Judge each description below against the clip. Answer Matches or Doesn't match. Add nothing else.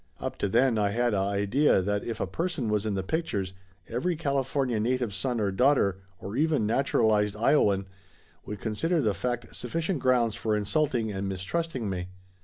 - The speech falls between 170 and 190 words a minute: Matches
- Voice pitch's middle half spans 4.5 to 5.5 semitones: Matches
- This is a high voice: Doesn't match